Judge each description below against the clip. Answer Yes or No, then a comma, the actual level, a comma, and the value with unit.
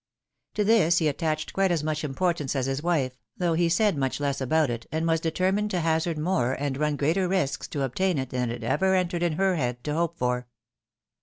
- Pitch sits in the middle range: Yes, medium, 160 Hz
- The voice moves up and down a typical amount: Yes, average, 4.5 semitones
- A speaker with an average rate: No, fast, 220 wpm